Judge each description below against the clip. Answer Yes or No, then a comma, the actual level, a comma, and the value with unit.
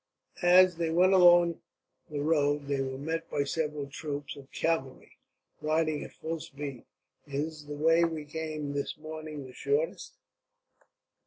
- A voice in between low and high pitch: Yes, medium, 155 Hz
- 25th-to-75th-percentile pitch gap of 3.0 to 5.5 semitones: No, narrow, 2.4 semitones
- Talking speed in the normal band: Yes, average, 145 wpm